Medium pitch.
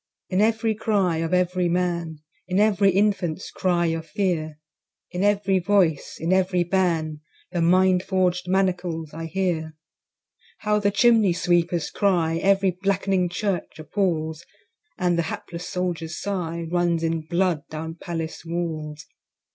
Yes: medium, 180 Hz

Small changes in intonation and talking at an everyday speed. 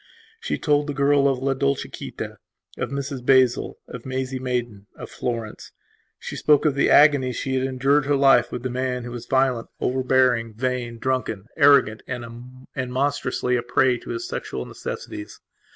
Yes: narrow, 2.1 semitones; average, 170 wpm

